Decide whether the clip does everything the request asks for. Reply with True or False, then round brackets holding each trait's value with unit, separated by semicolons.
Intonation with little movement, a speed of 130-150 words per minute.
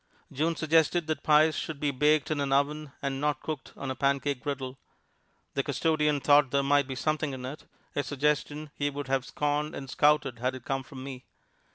False (1.9 semitones; 200 wpm)